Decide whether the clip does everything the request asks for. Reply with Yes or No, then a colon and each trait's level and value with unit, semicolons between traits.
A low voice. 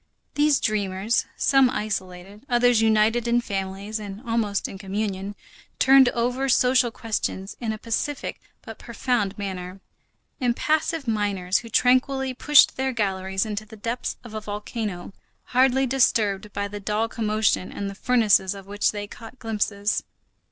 No: high, 215 Hz